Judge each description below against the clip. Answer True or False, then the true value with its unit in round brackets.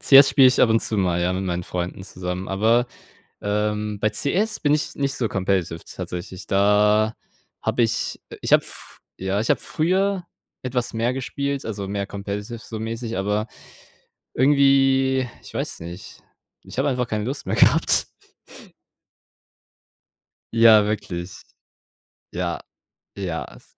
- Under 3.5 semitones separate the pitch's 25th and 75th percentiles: False (5.1 semitones)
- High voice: False (110 Hz)